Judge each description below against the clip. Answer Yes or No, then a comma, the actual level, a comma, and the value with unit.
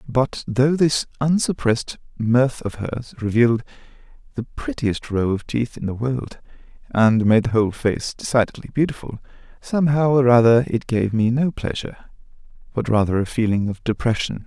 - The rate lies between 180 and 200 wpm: No, average, 155 wpm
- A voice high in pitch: No, low, 120 Hz